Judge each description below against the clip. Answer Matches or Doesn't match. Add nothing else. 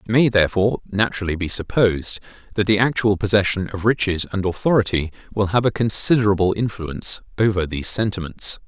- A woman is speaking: Doesn't match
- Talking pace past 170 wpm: Doesn't match